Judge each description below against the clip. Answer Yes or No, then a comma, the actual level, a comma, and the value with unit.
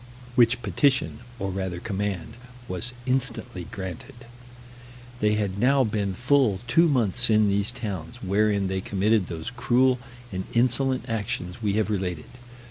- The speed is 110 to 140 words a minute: Yes, slow, 135 wpm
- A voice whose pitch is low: Yes, low, 105 Hz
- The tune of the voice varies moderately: Yes, average, 4.3 semitones